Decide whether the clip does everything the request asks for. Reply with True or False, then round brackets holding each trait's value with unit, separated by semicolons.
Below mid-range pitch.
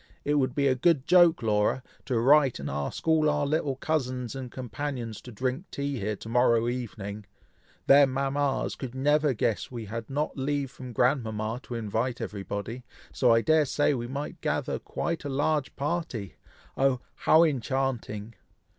True (130 Hz)